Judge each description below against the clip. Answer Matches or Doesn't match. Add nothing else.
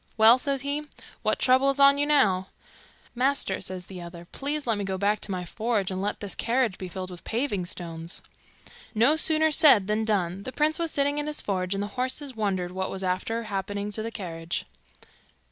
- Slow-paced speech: Doesn't match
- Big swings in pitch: Matches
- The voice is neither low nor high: Doesn't match